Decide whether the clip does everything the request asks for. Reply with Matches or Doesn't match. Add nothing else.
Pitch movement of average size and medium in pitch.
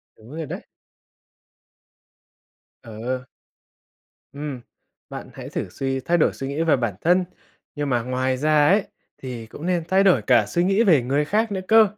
Doesn't match